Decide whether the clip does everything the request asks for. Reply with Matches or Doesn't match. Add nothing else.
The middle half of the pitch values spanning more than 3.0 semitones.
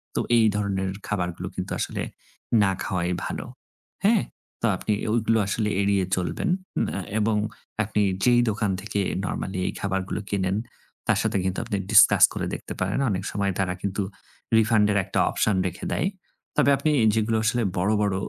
Doesn't match